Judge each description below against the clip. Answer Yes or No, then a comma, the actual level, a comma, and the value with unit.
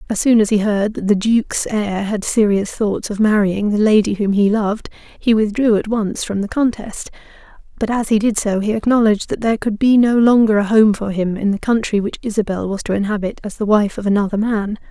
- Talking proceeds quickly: Yes, fast, 230 wpm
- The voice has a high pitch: Yes, high, 210 Hz